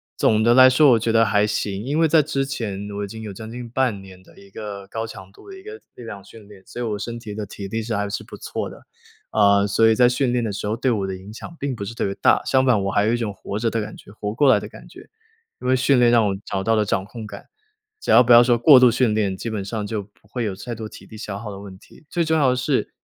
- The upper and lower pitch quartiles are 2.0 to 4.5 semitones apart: Yes, average, 3.2 semitones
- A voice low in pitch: Yes, low, 110 Hz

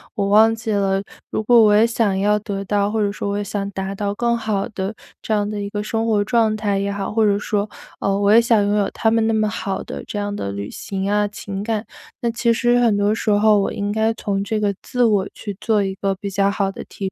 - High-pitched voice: Yes, high, 205 Hz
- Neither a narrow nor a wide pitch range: No, narrow, 1.7 semitones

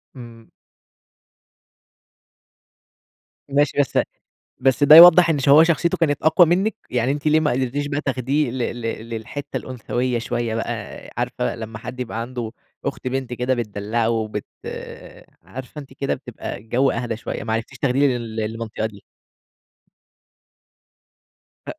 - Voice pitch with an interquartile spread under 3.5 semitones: No, average, 3.9 semitones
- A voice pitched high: No, low, 125 Hz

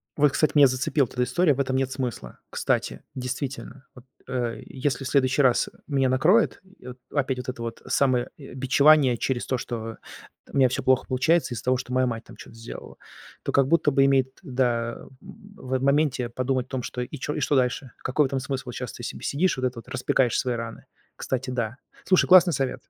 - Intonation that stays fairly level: Yes, narrow, 1.8 semitones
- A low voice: Yes, low, 130 Hz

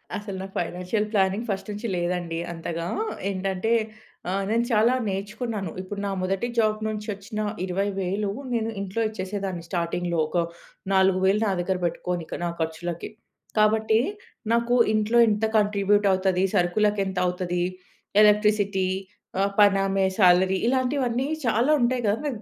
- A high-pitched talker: Yes, high, 195 Hz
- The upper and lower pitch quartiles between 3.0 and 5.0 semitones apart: No, narrow, 2.6 semitones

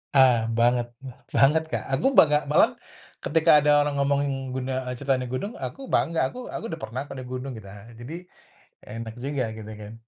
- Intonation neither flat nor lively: Yes, average, 3.4 semitones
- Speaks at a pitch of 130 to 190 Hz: Yes, low, 135 Hz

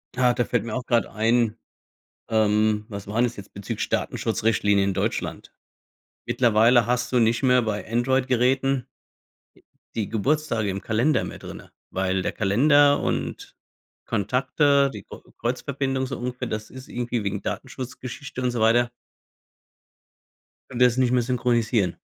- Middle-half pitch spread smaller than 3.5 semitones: Yes, average, 2.9 semitones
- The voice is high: No, low, 120 Hz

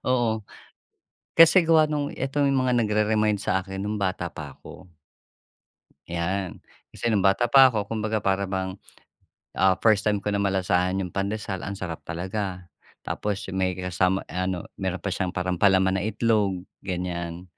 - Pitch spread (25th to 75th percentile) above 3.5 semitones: No, average, 2.7 semitones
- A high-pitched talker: No, very low, 95 Hz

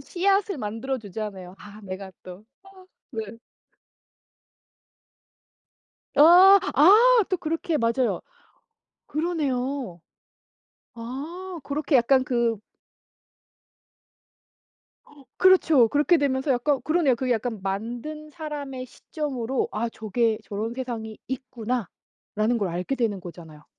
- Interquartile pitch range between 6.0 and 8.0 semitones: No, wide, 5.6 semitones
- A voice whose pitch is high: Yes, very high, 255 Hz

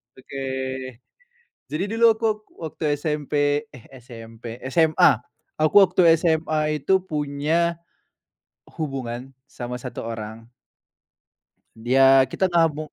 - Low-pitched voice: No, medium, 145 Hz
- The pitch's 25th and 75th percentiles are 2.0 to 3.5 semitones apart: No, average, 4.7 semitones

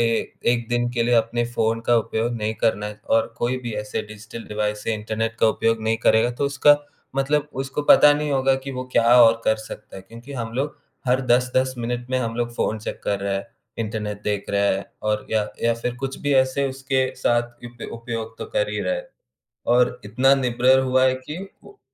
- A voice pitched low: Yes, low, 120 Hz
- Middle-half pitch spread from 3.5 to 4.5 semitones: No, average, 2.8 semitones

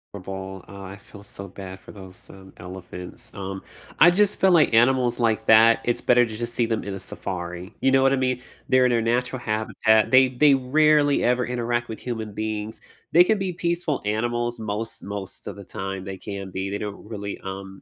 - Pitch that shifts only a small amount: No, average, 4.5 semitones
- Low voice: Yes, low, 110 Hz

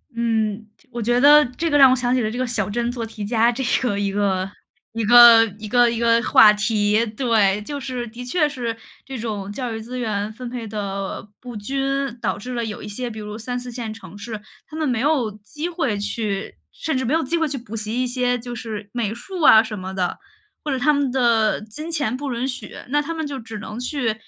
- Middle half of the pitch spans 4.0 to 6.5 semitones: No, average, 3.1 semitones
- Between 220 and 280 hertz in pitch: Yes, high, 235 Hz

